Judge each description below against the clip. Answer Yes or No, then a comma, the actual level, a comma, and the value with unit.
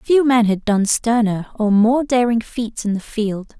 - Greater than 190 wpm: Yes, average, 200 wpm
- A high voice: Yes, high, 225 Hz